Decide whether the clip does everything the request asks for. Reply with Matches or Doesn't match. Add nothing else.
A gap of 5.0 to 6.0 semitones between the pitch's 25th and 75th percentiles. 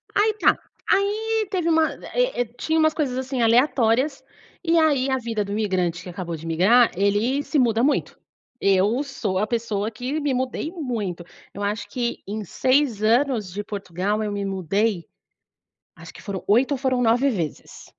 Matches